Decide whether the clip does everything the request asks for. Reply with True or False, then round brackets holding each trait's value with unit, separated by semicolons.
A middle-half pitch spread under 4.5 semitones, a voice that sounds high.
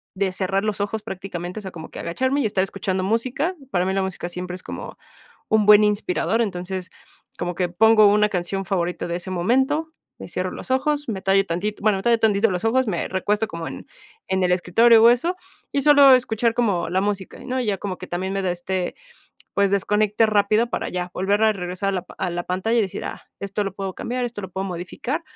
True (3.4 semitones; 200 Hz)